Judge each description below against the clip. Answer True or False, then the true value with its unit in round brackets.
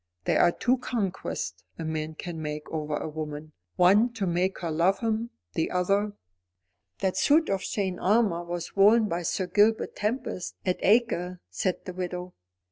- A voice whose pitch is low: False (180 Hz)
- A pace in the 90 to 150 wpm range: False (170 wpm)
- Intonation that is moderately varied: True (4.2 semitones)